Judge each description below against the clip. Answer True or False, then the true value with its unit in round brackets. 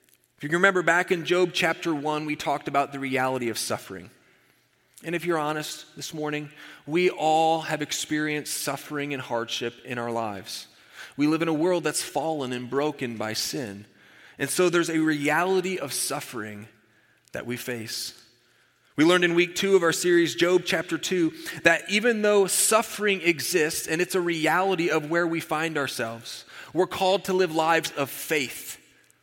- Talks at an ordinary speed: True (175 wpm)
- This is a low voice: False (155 Hz)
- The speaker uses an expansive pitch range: False (4.0 semitones)